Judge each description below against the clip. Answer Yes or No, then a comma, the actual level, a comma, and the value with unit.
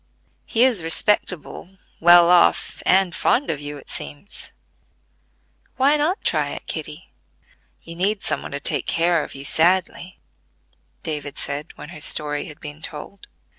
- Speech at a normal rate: Yes, average, 150 wpm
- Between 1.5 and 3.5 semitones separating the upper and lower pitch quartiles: No, average, 4.5 semitones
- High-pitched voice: No, medium, 170 Hz